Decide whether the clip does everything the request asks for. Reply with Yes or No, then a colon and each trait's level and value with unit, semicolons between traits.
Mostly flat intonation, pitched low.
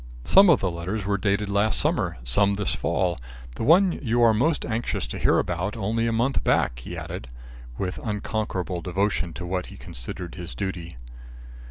No: average, 4.0 semitones; low, 100 Hz